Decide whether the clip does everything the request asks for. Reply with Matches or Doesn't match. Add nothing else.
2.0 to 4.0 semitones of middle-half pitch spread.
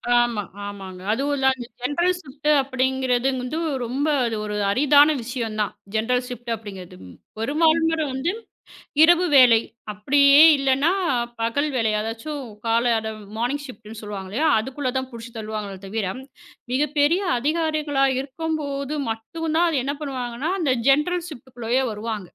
Doesn't match